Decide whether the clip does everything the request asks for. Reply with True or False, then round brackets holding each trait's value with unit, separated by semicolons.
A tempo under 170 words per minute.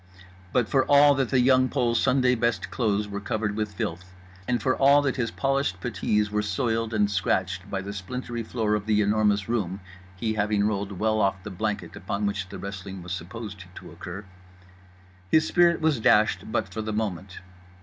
False (190 wpm)